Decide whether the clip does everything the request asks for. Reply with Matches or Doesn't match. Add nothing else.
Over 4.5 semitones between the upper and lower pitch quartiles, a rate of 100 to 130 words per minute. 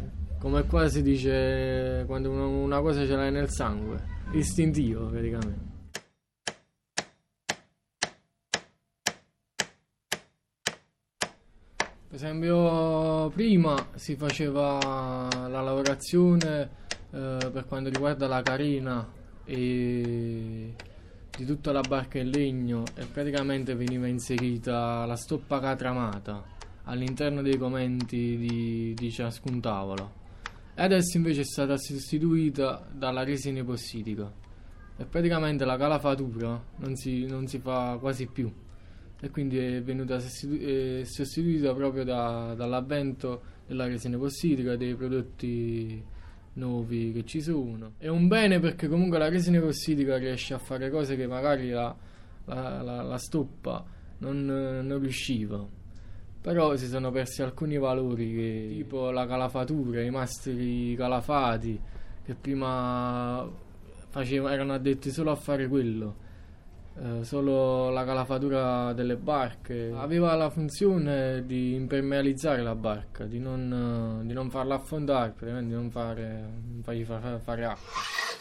Doesn't match